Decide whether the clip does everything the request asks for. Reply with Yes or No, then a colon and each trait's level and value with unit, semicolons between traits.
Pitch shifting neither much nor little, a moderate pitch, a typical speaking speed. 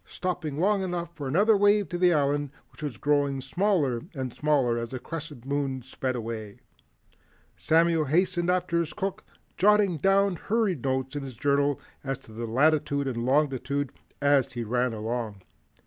Yes: average, 5.0 semitones; medium, 145 Hz; average, 160 wpm